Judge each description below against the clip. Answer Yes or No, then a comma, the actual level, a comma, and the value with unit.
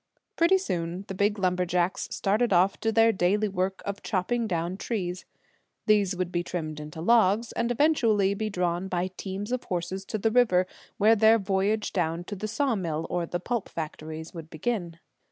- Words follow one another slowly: No, average, 175 wpm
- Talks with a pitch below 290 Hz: Yes, high, 190 Hz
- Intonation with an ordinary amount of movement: Yes, average, 3.7 semitones